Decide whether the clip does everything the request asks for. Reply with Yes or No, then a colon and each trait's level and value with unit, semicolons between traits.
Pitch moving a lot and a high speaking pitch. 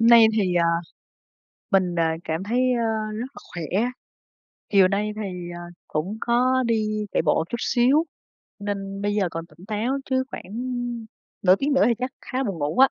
No: average, 4.6 semitones; high, 210 Hz